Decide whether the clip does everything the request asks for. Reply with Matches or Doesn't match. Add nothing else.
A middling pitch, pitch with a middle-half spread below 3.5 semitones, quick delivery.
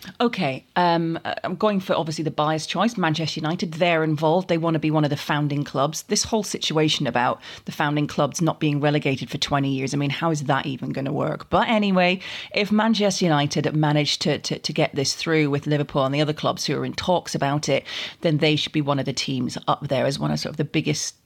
Matches